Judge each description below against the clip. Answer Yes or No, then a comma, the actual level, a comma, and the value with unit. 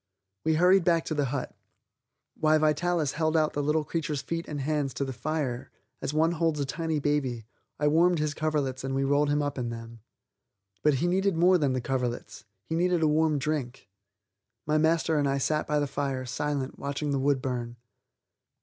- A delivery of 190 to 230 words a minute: Yes, average, 195 wpm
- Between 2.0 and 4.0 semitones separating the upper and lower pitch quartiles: Yes, average, 2.8 semitones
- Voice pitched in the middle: Yes, medium, 150 Hz